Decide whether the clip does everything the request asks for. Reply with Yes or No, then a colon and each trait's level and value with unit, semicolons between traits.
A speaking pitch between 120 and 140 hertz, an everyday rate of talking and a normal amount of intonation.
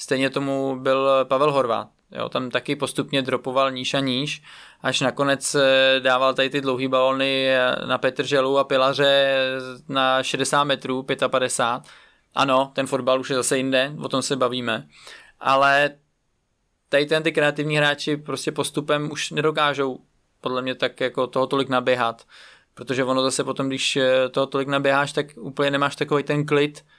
No: low, 135 Hz; average, 155 wpm; narrow, 1.4 semitones